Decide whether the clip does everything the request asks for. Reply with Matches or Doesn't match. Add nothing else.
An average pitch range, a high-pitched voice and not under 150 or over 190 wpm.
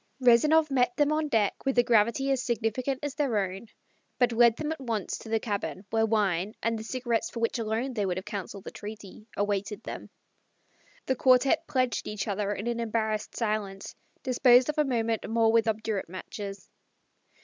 Matches